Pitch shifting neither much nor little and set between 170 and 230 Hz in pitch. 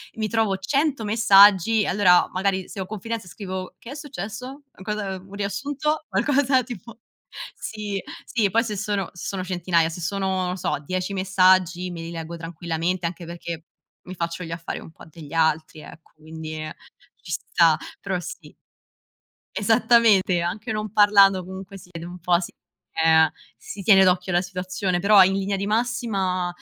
Yes: average, 3.2 semitones; high, 190 Hz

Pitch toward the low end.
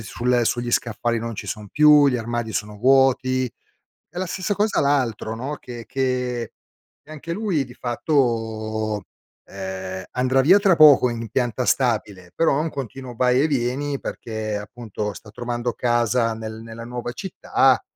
Yes: low, 120 Hz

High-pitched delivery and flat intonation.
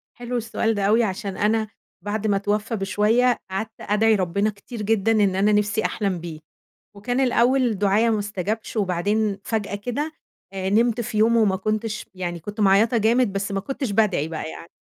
Yes: high, 210 Hz; narrow, 2.3 semitones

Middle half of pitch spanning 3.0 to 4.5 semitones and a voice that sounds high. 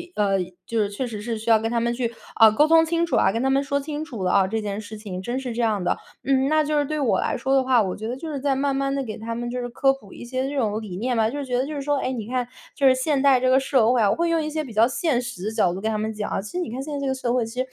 Yes: average, 3.8 semitones; very high, 250 Hz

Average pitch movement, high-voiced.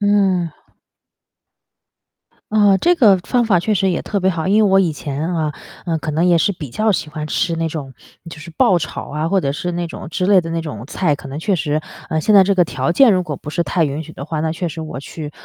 No: average, 3.8 semitones; medium, 170 Hz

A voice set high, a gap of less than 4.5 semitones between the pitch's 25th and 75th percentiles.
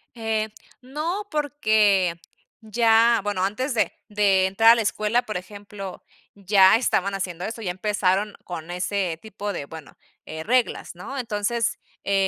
Yes: high, 205 Hz; average, 3.2 semitones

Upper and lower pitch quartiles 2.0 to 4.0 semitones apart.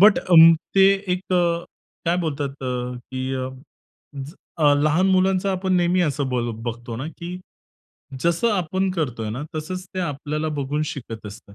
No: wide, 5.5 semitones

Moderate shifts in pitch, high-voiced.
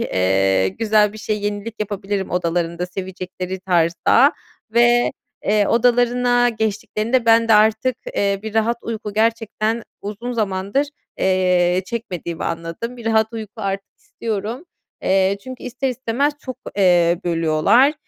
Yes: average, 3.8 semitones; high, 210 Hz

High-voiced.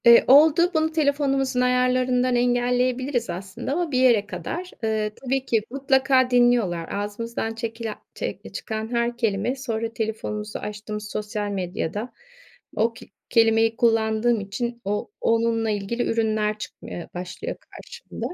Yes: high, 230 Hz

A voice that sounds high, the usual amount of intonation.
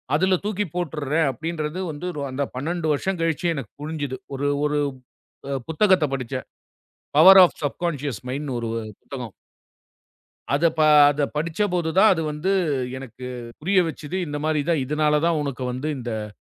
No: medium, 150 Hz; average, 3.9 semitones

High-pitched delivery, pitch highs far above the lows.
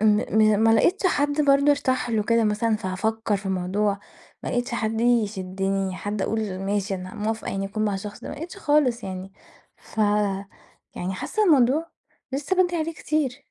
Yes: high, 220 Hz; wide, 5.8 semitones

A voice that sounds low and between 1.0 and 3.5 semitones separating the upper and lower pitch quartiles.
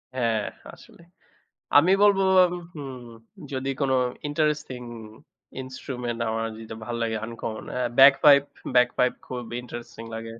Yes: low, 125 Hz; average, 3.2 semitones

